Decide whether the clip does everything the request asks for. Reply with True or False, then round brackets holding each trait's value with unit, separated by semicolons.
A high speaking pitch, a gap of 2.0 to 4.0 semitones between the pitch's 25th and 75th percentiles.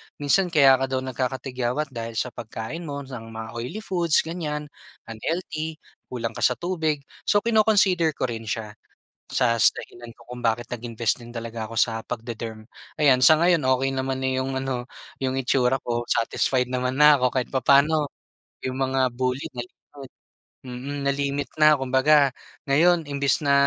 False (130 Hz; 3.5 semitones)